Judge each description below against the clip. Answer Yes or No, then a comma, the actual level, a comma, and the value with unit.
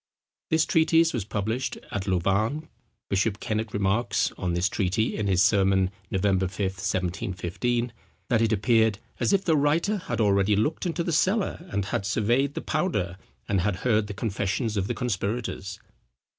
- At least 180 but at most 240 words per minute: No, average, 160 wpm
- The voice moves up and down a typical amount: Yes, average, 4.5 semitones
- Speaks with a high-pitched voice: No, low, 105 Hz